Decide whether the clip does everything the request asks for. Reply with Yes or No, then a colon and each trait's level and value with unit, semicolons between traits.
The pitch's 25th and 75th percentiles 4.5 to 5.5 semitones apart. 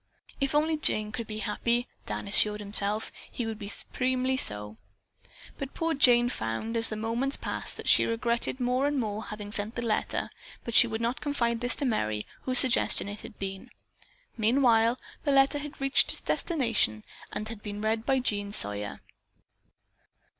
No: average, 3.6 semitones